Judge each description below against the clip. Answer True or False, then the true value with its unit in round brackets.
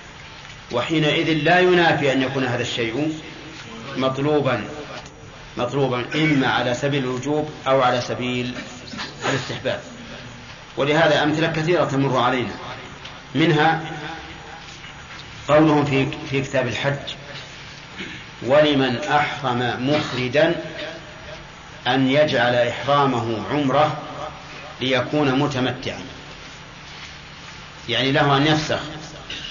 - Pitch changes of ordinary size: True (3.1 semitones)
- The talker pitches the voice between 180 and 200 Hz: False (145 Hz)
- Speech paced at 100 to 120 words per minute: False (85 wpm)